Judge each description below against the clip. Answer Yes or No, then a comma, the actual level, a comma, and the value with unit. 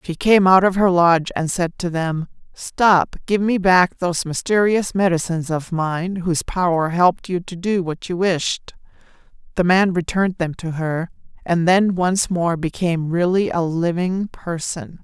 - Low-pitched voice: No, medium, 175 Hz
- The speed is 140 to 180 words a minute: Yes, average, 170 wpm